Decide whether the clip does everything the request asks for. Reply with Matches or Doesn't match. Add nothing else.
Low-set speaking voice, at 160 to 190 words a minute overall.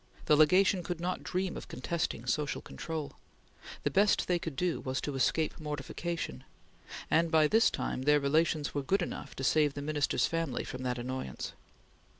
Doesn't match